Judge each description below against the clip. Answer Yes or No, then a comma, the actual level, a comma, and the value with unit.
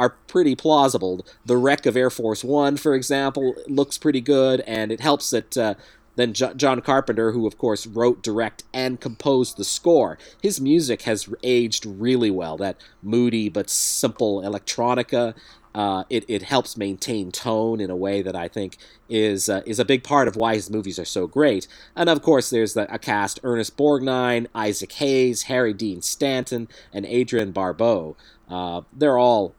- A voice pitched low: Yes, low, 120 Hz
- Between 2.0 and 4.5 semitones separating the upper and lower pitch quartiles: Yes, average, 3.8 semitones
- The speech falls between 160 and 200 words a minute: Yes, average, 180 wpm